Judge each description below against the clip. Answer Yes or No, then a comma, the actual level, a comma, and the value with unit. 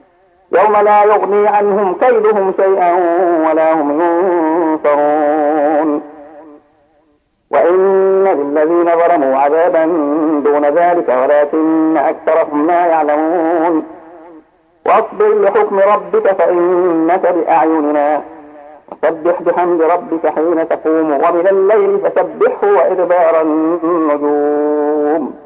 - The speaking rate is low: No, average, 80 wpm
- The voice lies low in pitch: No, medium, 165 Hz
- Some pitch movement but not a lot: Yes, average, 3.2 semitones